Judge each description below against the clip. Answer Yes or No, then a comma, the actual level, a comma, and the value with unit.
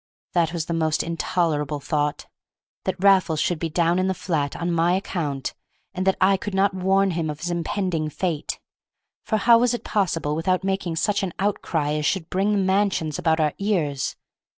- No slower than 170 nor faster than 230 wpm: Yes, average, 190 wpm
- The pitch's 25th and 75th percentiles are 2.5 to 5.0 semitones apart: Yes, average, 3.5 semitones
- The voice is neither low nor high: Yes, medium, 175 Hz